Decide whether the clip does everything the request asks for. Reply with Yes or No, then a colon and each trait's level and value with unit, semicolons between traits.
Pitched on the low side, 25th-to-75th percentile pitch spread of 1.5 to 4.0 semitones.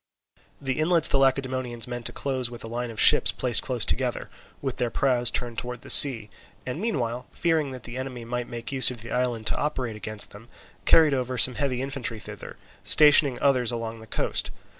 Yes: low, 125 Hz; narrow, 2.4 semitones